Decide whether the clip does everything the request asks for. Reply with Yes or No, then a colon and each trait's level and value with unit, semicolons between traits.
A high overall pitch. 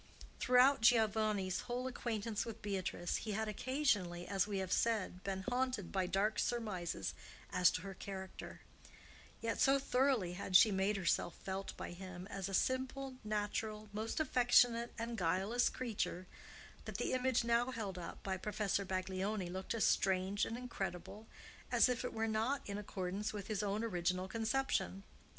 Yes: high, 210 Hz